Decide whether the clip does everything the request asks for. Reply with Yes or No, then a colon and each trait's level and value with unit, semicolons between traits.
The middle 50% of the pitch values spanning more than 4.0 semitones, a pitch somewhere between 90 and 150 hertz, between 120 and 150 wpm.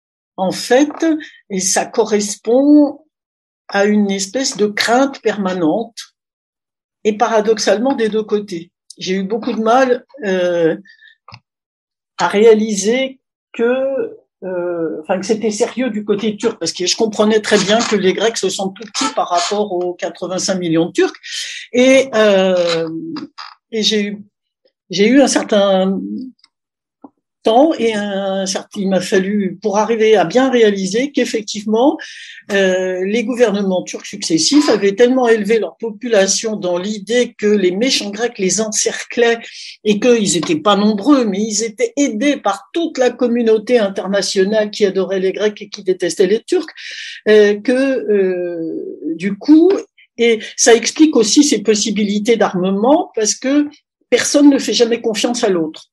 No: average, 4.4 semitones; high, 220 Hz; slow, 145 wpm